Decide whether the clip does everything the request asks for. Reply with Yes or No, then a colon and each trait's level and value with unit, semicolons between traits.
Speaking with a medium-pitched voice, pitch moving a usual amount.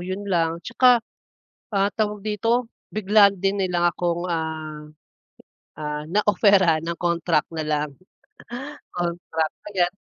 Yes: medium, 175 Hz; average, 3.8 semitones